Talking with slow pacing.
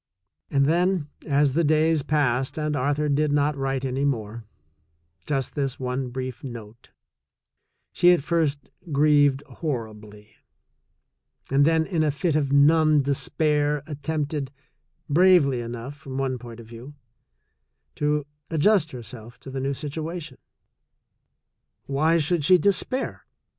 Yes: slow, 130 wpm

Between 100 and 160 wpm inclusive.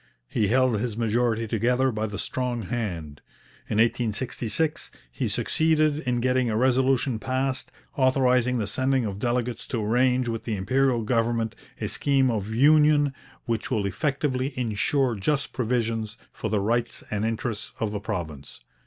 Yes: average, 150 wpm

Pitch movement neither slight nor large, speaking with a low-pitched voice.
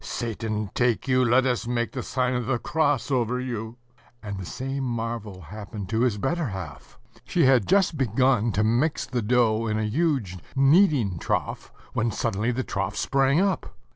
Yes: average, 3.7 semitones; low, 120 Hz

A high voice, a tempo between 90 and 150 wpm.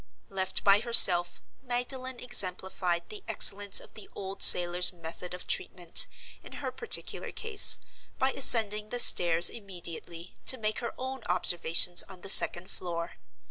Yes: high, 195 Hz; average, 140 wpm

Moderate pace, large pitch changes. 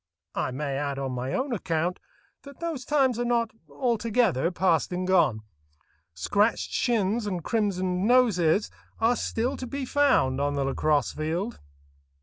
Yes: average, 145 wpm; wide, 7.8 semitones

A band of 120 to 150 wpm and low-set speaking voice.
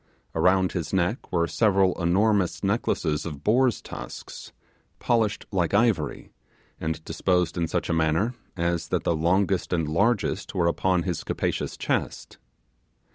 Yes: slow, 135 wpm; very low, 90 Hz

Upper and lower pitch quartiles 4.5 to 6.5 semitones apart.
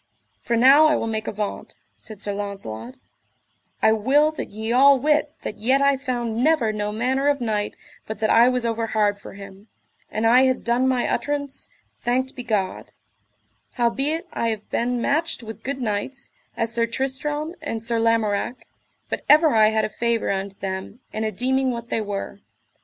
No: average, 3.7 semitones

